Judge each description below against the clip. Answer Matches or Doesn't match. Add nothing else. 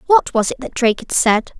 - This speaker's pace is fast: Matches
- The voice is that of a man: Doesn't match